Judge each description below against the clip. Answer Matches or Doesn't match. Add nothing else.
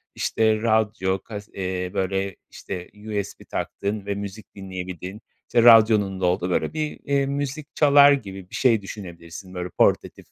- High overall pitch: Doesn't match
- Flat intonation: Doesn't match